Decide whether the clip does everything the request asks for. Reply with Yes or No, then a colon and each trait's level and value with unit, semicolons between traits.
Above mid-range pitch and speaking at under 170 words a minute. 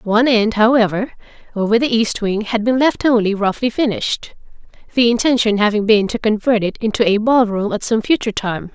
No: high, 220 Hz; average, 190 wpm